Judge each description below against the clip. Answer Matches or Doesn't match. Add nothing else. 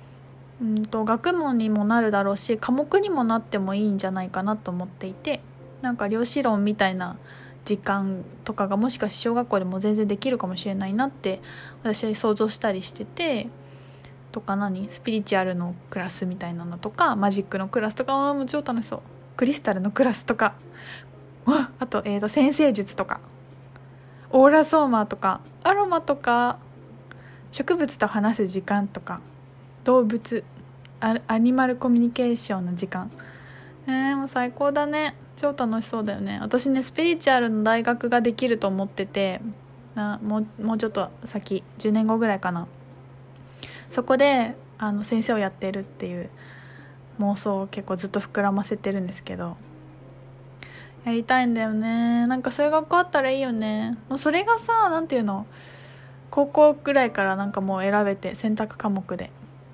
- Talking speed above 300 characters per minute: Matches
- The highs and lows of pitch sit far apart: Doesn't match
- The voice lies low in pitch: Doesn't match